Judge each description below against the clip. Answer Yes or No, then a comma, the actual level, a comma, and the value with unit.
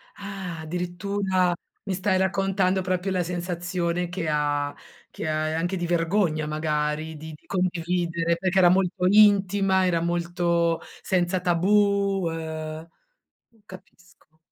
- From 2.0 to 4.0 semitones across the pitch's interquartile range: Yes, narrow, 2.4 semitones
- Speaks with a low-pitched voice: No, medium, 175 Hz